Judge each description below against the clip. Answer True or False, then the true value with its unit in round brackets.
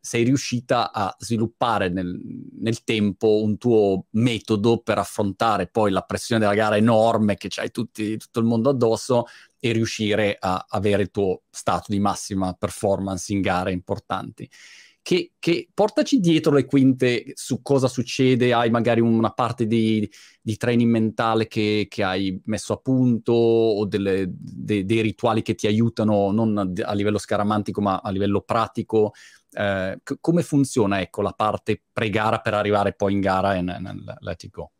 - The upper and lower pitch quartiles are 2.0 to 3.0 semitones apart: True (2.7 semitones)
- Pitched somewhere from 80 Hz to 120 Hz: True (110 Hz)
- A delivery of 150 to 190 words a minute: True (165 wpm)